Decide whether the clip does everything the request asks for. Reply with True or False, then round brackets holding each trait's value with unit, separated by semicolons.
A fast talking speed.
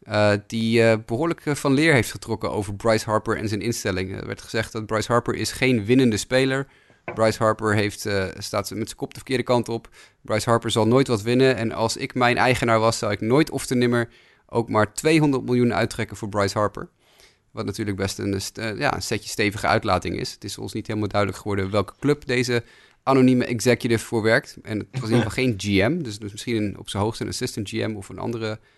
True (230 wpm)